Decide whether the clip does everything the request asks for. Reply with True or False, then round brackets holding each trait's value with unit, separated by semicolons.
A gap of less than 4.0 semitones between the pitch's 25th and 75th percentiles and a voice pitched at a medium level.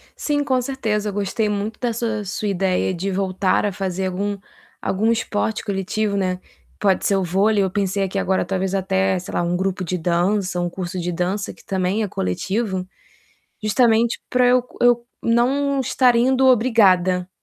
False (3.3 semitones; 200 Hz)